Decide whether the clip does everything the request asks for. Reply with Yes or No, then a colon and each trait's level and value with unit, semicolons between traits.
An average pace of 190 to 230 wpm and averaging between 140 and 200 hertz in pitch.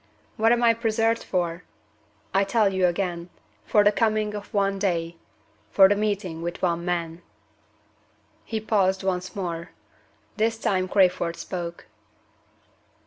No: slow, 135 wpm; high, 190 Hz